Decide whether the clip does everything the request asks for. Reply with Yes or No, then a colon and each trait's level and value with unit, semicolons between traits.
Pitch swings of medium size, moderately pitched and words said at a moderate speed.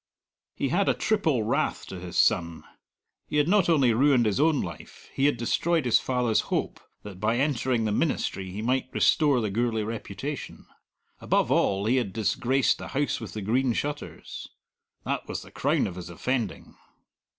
No: average, 4.8 semitones; low, 120 Hz; average, 175 wpm